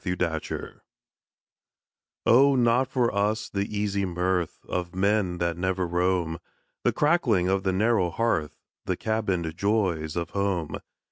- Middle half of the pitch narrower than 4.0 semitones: Yes, average, 3.6 semitones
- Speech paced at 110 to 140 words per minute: Yes, slow, 135 wpm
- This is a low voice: Yes, very low, 95 Hz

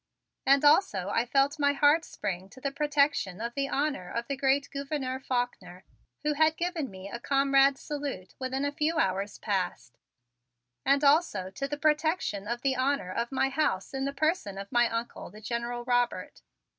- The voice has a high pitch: Yes, very high, 270 Hz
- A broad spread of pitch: No, average, 4.1 semitones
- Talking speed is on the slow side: No, average, 175 wpm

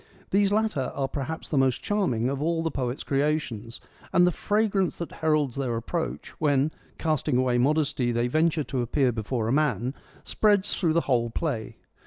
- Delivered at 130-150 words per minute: No, average, 175 wpm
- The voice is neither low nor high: Yes, medium, 145 Hz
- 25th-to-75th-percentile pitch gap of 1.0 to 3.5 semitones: No, average, 4.7 semitones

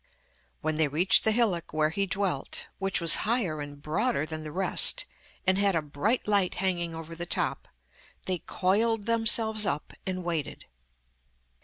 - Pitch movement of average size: Yes, average, 4.6 semitones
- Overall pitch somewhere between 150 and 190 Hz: Yes, medium, 185 Hz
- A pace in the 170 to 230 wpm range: No, average, 160 wpm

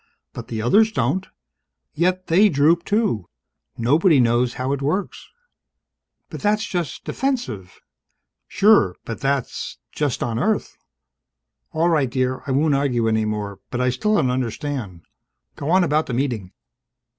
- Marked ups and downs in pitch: Yes, wide, 6.7 semitones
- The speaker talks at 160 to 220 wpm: No, average, 145 wpm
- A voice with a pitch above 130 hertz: Yes, medium, 140 Hz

